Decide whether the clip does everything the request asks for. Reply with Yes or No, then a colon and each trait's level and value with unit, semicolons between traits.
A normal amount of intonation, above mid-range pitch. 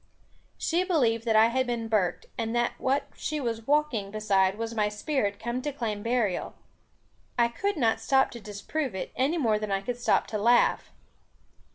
Yes: average, 3.6 semitones; high, 230 Hz